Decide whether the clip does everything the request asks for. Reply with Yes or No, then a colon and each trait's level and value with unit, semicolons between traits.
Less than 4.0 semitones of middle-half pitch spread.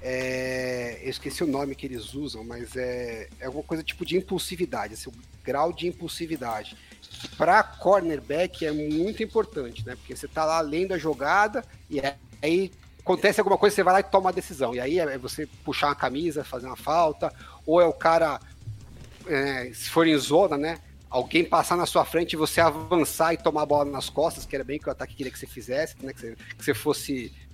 No: average, 4.7 semitones